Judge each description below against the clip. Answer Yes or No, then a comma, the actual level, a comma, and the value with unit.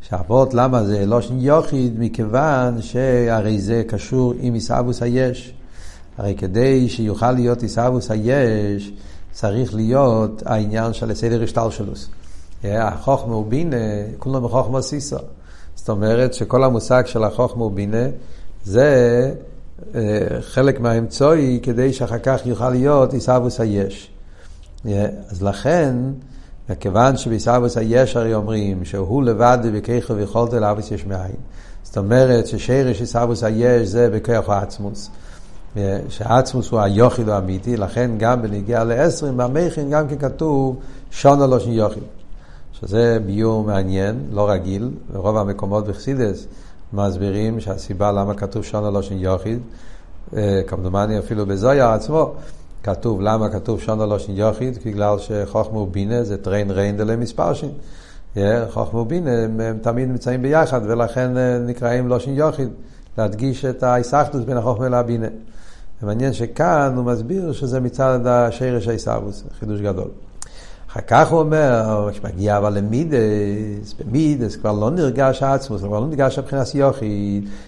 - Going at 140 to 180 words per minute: No, average, 130 wpm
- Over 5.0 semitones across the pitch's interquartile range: No, average, 3.7 semitones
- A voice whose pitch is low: Yes, low, 115 Hz